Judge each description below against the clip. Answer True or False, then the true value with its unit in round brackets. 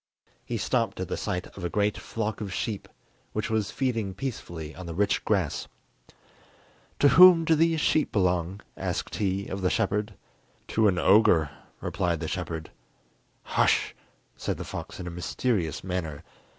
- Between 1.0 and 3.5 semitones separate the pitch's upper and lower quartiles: False (4.0 semitones)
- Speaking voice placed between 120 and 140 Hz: False (100 Hz)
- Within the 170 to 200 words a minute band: False (160 wpm)